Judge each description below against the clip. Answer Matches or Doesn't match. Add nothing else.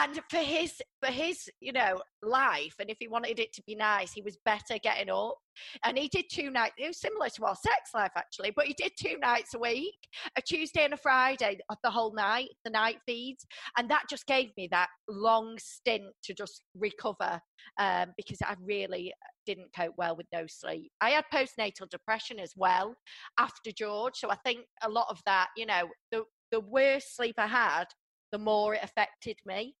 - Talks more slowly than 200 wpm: Doesn't match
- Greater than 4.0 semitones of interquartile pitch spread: Matches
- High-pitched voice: Matches